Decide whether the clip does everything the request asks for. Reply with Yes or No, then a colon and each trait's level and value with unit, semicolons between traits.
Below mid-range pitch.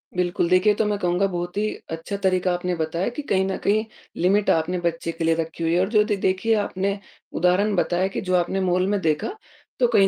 No: medium, 185 Hz